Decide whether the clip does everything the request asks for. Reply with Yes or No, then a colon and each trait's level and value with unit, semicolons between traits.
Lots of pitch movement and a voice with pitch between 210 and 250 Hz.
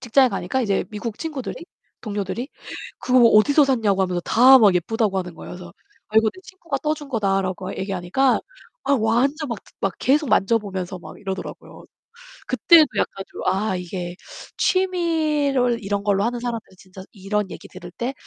Yes: wide, 5.8 semitones; high, 220 Hz